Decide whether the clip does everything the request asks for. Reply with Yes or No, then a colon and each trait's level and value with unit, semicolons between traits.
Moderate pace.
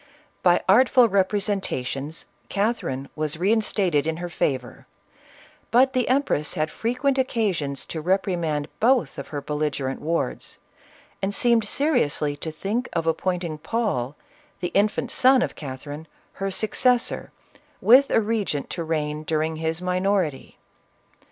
No: slow, 130 wpm